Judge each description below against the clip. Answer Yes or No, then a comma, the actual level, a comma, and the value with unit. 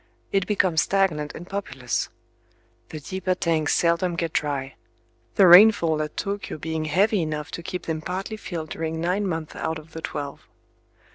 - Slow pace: No, average, 155 wpm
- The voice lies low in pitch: No, medium, 165 Hz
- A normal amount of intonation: Yes, average, 3.2 semitones